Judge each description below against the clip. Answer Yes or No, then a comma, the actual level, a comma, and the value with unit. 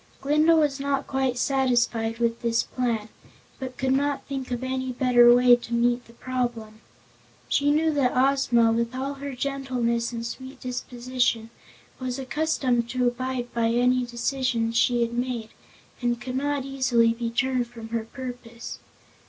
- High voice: Yes, very high, 250 Hz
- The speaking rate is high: No, average, 155 wpm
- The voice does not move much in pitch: Yes, narrow, 2.1 semitones